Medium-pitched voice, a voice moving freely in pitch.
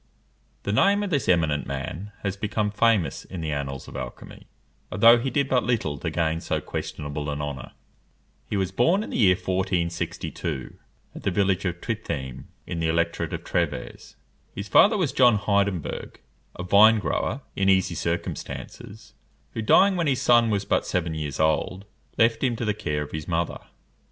No: very low, 95 Hz; wide, 6.0 semitones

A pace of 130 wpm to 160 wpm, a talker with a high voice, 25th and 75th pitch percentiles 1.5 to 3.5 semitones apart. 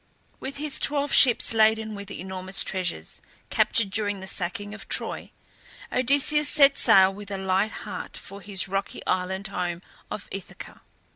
Yes: average, 150 wpm; high, 200 Hz; average, 2.9 semitones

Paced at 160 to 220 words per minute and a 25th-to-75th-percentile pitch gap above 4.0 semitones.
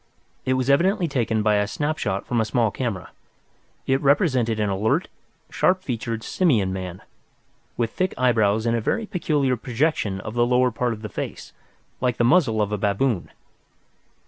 Yes: average, 170 wpm; average, 4.4 semitones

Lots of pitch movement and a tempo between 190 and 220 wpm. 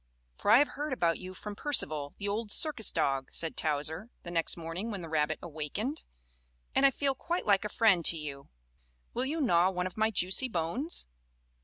Yes: wide, 6.6 semitones; average, 195 wpm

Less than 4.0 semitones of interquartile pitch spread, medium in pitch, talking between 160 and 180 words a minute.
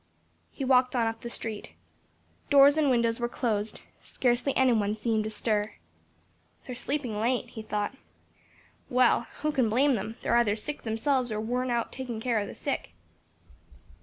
No: average, 2.9 semitones; high, 235 Hz; average, 165 wpm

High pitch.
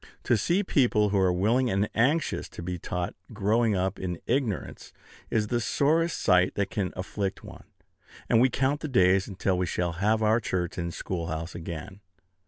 No: low, 100 Hz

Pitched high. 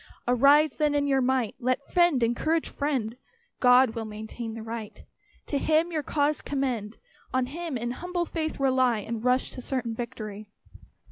Yes: very high, 255 Hz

